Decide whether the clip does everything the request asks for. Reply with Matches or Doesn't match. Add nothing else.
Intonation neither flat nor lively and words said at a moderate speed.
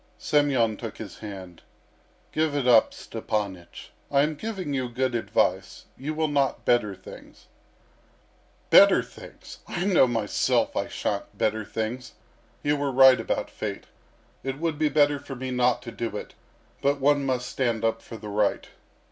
Matches